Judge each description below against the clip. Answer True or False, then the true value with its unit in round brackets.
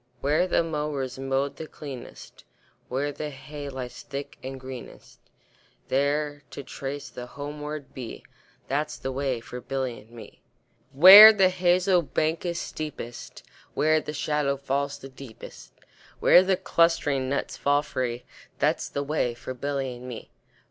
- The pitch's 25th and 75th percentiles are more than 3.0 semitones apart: False (2.6 semitones)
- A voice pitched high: False (140 Hz)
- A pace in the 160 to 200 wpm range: False (150 wpm)